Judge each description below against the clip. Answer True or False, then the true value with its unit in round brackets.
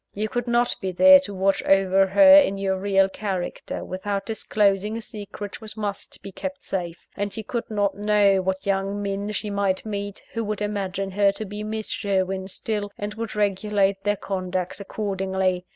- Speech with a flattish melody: True (1.6 semitones)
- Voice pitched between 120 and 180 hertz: False (200 Hz)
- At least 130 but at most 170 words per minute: False (185 wpm)